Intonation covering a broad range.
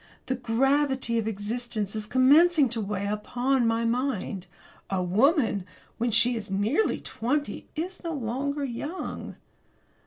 No: average, 4.4 semitones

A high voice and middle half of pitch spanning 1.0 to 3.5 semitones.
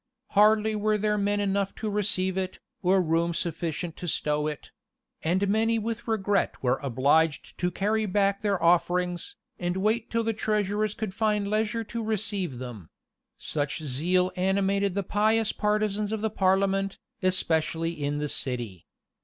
No: high, 195 Hz; average, 3.9 semitones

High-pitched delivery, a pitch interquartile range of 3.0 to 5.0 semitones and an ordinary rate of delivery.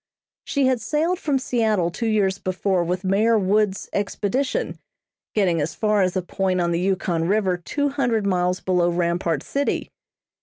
Yes: high, 195 Hz; average, 4.0 semitones; average, 160 wpm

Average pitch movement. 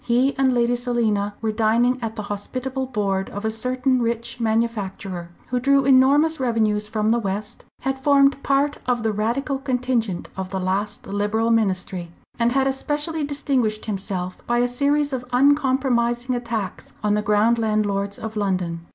Yes: average, 4.0 semitones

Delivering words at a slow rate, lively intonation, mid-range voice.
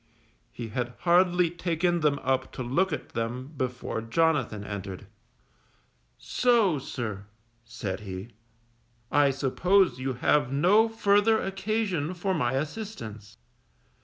Yes: slow, 115 wpm; wide, 7.2 semitones; medium, 145 Hz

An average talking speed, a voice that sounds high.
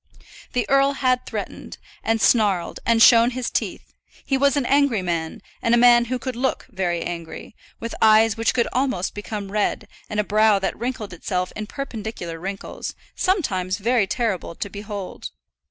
Yes: average, 170 wpm; high, 220 Hz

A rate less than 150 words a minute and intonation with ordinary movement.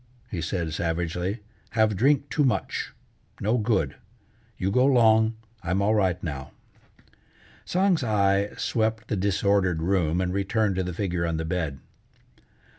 Yes: average, 140 wpm; average, 4.0 semitones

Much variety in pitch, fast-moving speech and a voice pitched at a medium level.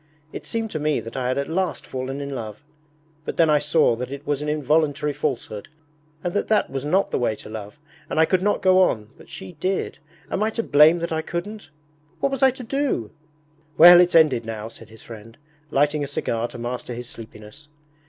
Yes: wide, 6.4 semitones; fast, 220 wpm; medium, 145 Hz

